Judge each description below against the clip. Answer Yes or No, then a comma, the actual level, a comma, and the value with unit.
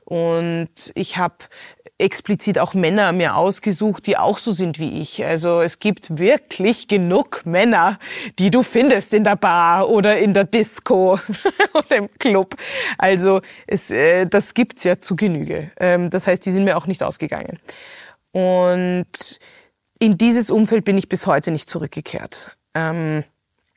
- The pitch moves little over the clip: No, average, 3.8 semitones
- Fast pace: No, average, 145 wpm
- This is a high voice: Yes, high, 195 Hz